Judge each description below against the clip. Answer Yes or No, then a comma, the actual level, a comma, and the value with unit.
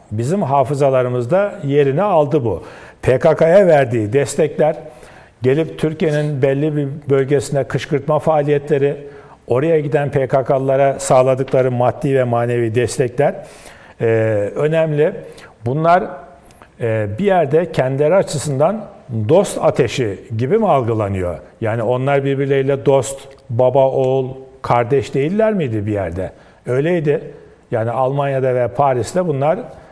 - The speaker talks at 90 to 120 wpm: Yes, average, 105 wpm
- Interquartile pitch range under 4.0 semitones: Yes, average, 3.4 semitones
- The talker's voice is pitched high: No, medium, 140 Hz